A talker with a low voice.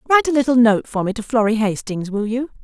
No: high, 230 Hz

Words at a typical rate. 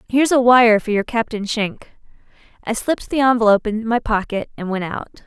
Yes: average, 195 wpm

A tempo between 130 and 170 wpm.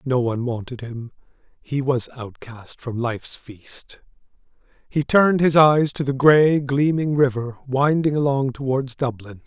Yes: average, 145 wpm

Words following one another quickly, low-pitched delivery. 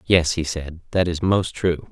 Yes: fast, 220 wpm; very low, 85 Hz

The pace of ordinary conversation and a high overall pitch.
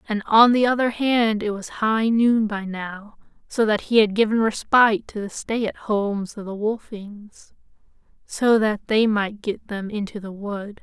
Yes: average, 190 wpm; high, 215 Hz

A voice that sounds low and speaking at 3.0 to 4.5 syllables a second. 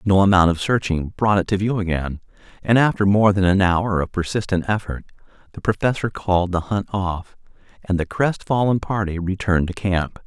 No: very low, 95 Hz; 5.3 syllables/s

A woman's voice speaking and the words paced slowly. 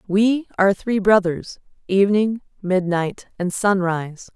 Yes: female; slow, 95 wpm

